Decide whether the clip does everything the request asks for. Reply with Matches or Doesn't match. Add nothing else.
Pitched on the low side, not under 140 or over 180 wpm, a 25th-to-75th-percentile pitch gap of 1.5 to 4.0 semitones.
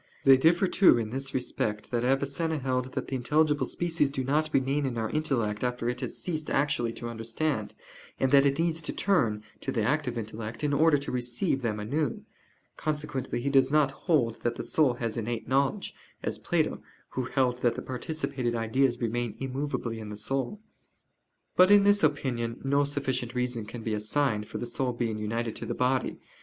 Doesn't match